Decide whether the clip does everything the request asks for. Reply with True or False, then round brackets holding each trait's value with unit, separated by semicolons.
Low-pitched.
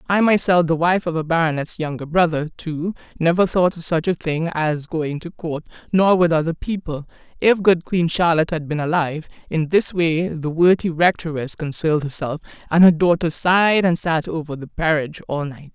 False (165 Hz)